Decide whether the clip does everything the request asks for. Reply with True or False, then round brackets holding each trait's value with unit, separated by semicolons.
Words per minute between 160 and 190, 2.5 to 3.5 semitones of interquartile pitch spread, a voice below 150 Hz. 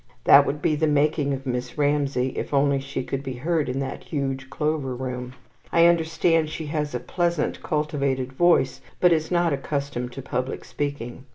True (180 wpm; 2.8 semitones; 140 Hz)